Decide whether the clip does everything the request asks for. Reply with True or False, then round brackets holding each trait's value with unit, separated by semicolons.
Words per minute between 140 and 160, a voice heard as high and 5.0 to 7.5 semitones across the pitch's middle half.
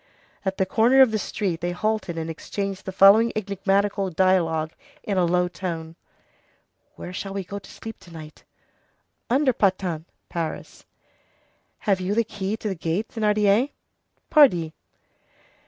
False (145 wpm; 195 Hz; 3.3 semitones)